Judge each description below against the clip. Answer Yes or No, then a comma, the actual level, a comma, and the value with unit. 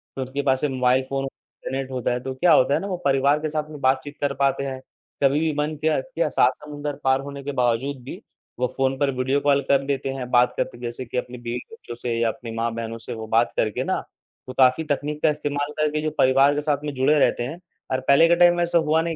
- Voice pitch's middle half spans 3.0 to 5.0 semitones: No, narrow, 2.6 semitones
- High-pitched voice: No, low, 135 Hz